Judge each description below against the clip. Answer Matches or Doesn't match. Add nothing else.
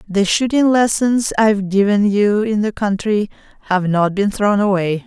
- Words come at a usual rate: Matches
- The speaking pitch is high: Matches